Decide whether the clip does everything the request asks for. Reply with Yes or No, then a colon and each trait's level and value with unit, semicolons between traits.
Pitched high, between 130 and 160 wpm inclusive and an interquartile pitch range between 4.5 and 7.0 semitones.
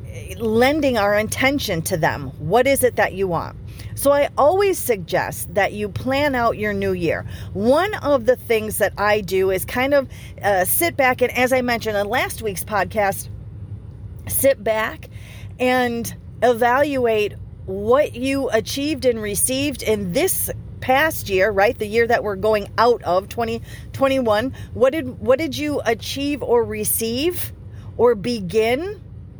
Yes: high, 225 Hz; average, 155 wpm; wide, 5.6 semitones